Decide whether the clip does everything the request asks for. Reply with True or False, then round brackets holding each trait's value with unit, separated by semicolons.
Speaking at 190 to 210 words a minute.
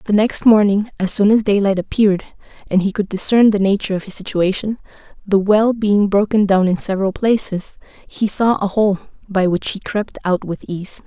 True (195 wpm)